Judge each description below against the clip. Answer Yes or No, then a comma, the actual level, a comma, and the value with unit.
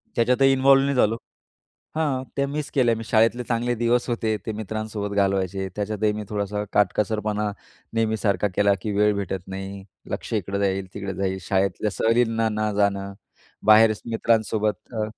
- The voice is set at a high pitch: No, low, 110 Hz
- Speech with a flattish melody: Yes, narrow, 2.3 semitones